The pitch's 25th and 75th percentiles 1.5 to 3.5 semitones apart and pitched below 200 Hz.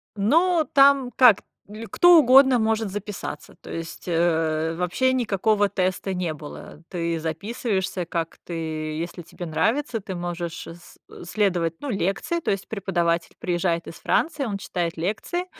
No: average, 5.1 semitones; high, 190 Hz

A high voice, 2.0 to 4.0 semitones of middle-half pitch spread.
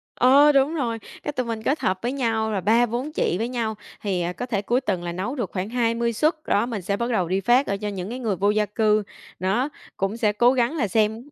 Yes: high, 225 Hz; average, 3.6 semitones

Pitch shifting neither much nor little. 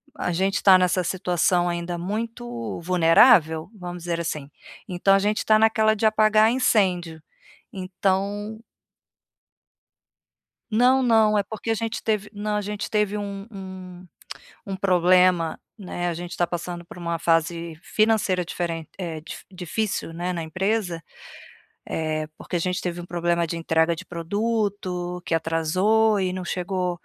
Yes: average, 3.4 semitones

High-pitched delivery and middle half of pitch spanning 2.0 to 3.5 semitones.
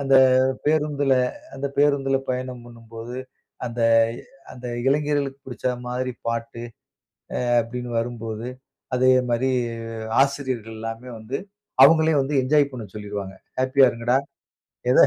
No: low, 125 Hz; average, 2.9 semitones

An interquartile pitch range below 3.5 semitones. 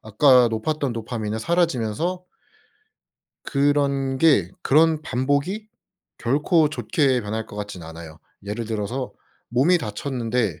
No: average, 5.3 semitones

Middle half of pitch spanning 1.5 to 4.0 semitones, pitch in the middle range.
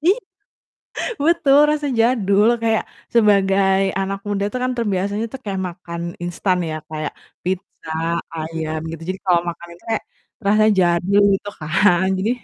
No: average, 3.6 semitones; high, 195 Hz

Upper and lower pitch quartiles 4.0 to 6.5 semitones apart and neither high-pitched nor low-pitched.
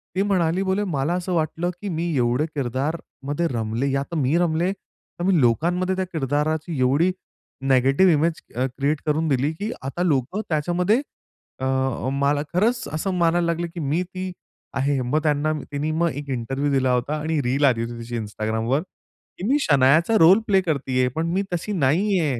Yes: average, 4.6 semitones; medium, 155 Hz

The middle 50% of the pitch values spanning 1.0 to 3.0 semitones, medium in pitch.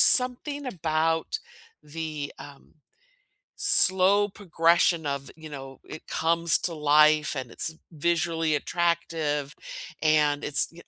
Yes: narrow, 2.4 semitones; medium, 160 Hz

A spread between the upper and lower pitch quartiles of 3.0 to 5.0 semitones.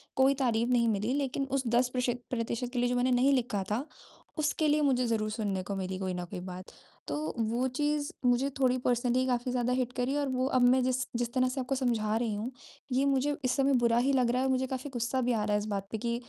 No: narrow, 2.6 semitones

